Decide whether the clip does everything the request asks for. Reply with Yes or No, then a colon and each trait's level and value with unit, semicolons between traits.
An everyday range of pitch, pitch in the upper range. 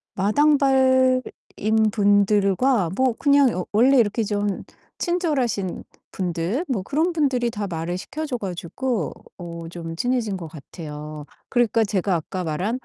No: wide, 6.5 semitones; high, 210 Hz